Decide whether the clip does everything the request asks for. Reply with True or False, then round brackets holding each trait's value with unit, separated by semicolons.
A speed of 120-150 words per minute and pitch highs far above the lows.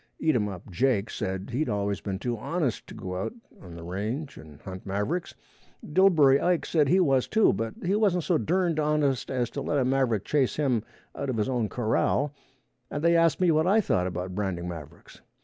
False (200 wpm; 7.9 semitones)